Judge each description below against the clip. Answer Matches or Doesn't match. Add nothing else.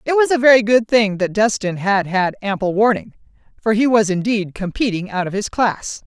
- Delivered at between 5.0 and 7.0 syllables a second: Matches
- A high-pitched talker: Matches